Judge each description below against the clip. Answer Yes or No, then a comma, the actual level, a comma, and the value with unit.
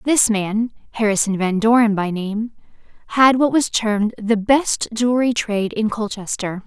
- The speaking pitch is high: Yes, high, 220 Hz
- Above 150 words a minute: No, slow, 135 wpm